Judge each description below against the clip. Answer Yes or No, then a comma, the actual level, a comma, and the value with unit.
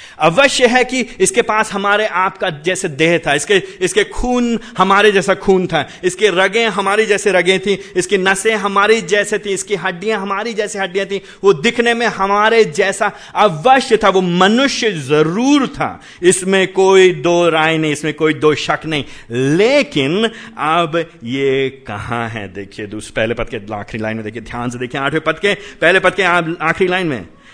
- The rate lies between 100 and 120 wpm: No, average, 175 wpm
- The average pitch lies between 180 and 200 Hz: Yes, high, 190 Hz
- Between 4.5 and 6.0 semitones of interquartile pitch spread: Yes, average, 5.2 semitones